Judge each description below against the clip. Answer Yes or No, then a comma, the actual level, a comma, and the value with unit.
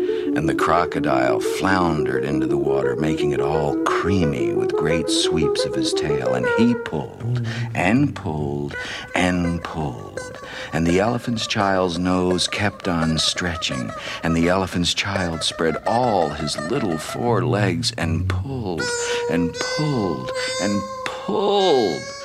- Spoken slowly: Yes, slow, 130 wpm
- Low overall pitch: Yes, low, 120 Hz